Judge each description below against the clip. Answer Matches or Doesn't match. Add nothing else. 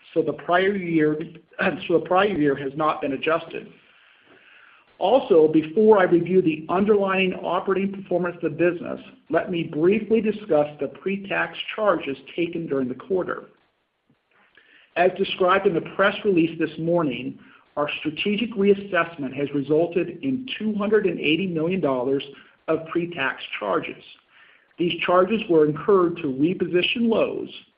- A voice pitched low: Doesn't match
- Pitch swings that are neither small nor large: Matches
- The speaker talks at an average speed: Doesn't match